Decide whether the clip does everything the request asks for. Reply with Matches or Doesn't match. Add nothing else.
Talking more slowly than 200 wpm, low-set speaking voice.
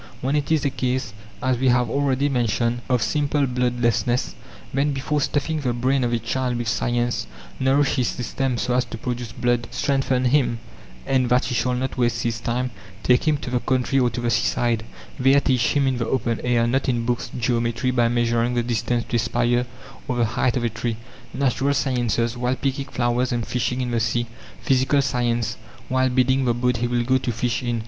Doesn't match